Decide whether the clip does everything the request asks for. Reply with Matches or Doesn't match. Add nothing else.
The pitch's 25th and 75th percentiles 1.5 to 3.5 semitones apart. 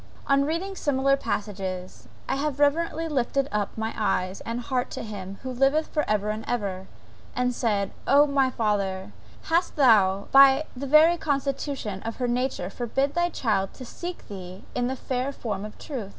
Doesn't match